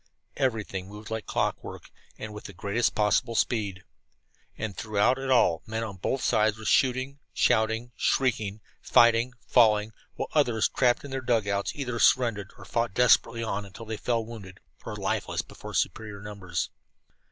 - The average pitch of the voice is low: Yes, low, 110 Hz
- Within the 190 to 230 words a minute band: No, average, 160 wpm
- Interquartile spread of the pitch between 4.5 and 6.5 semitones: No, average, 2.8 semitones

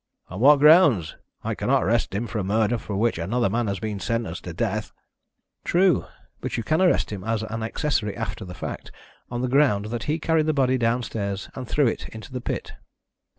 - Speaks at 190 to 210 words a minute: Yes, average, 200 wpm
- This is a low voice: Yes, low, 115 Hz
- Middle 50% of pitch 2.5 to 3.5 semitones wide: No, average, 4.4 semitones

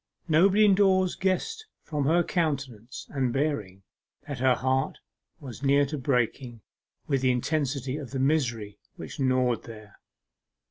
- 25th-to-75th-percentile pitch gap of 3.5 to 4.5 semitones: Yes, average, 4.0 semitones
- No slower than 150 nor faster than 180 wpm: No, slow, 135 wpm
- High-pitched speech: No, low, 135 Hz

